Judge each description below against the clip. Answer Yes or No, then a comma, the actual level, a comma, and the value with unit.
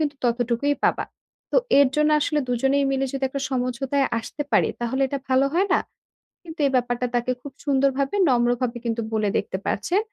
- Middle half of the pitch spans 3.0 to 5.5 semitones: No, narrow, 2.6 semitones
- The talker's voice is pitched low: No, very high, 265 Hz